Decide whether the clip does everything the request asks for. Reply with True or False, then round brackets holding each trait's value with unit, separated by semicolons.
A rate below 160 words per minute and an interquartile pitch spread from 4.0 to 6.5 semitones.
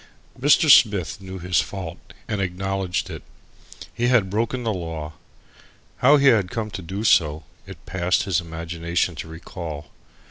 True (150 wpm; 4.3 semitones)